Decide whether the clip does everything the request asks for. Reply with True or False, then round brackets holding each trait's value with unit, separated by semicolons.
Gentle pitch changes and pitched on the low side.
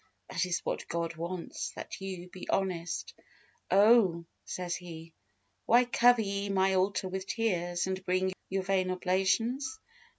False (1.9 semitones; 185 Hz)